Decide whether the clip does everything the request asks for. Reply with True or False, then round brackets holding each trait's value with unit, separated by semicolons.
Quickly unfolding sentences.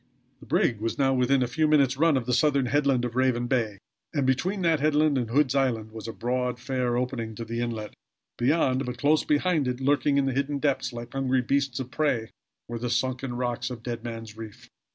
True (215 wpm)